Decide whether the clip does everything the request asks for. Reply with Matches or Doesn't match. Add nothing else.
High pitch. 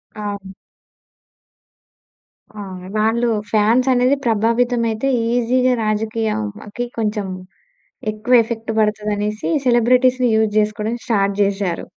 Matches